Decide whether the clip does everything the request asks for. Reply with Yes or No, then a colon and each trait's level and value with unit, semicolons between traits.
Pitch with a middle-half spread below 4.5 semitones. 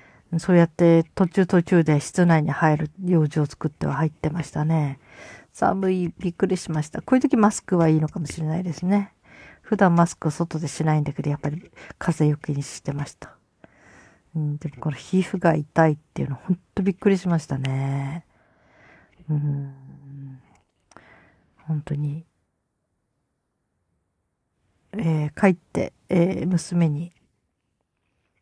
Yes: average, 3.2 semitones